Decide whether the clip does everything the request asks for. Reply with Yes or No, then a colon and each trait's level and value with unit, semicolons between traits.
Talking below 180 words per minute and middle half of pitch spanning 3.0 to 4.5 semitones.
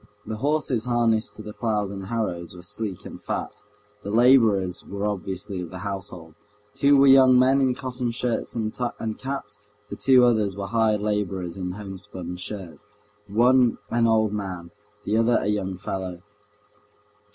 Yes: average, 160 wpm; average, 3.9 semitones